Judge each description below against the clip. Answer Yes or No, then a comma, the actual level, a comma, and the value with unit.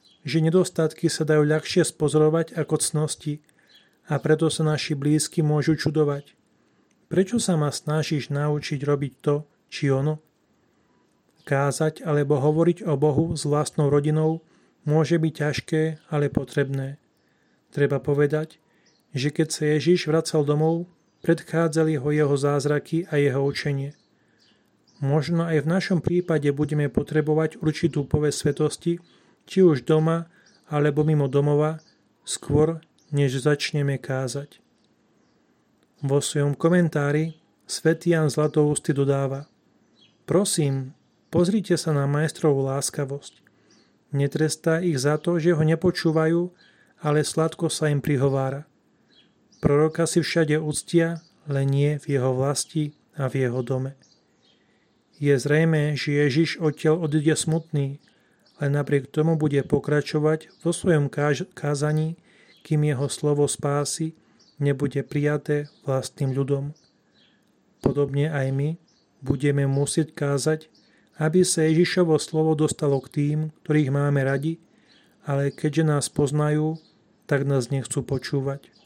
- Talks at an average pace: Yes, average, 120 wpm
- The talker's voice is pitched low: No, medium, 150 Hz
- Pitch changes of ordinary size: No, narrow, 2.0 semitones